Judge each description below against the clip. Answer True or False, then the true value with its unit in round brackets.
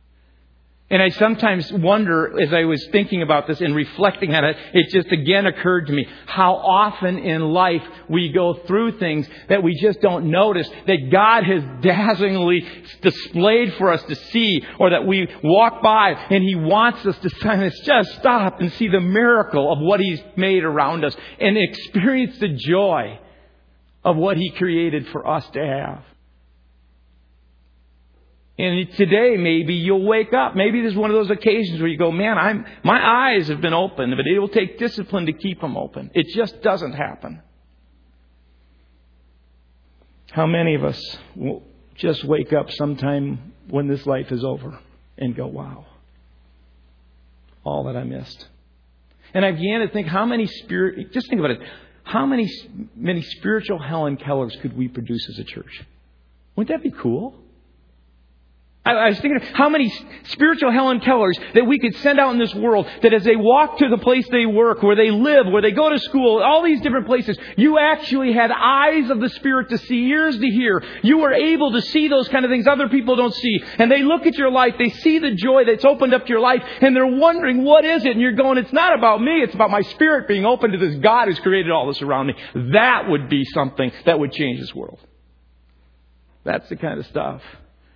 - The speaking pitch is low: False (190 Hz)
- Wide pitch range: True (9.0 semitones)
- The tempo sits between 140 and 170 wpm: False (190 wpm)